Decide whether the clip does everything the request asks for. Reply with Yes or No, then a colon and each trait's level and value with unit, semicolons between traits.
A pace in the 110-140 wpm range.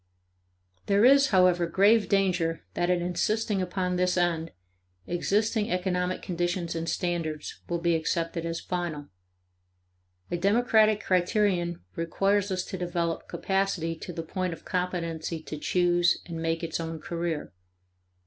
Yes: slow, 135 wpm